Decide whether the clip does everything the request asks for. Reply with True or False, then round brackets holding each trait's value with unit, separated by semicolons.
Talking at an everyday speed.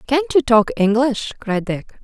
True (175 wpm)